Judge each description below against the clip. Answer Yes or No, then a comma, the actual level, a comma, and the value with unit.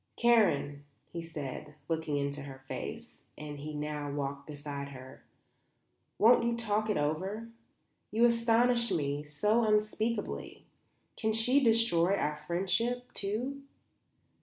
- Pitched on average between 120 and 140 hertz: No, medium, 180 Hz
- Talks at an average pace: No, slow, 120 wpm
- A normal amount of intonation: No, wide, 7.6 semitones